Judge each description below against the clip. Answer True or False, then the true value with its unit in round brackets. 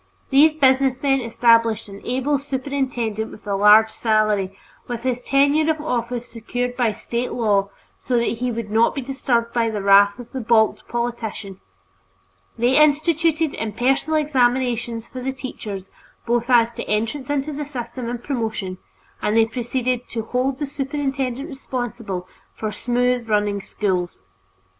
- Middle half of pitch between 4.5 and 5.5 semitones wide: False (3.2 semitones)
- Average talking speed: True (150 wpm)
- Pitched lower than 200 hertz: False (240 Hz)